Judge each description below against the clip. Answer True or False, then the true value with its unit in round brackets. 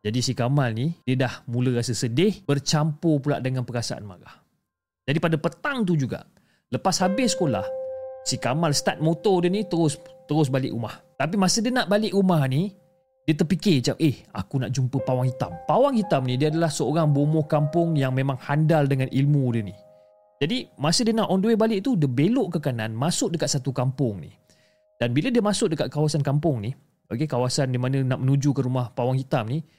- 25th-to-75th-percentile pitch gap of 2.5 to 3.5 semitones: False (5.2 semitones)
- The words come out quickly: True (200 wpm)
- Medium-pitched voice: True (145 Hz)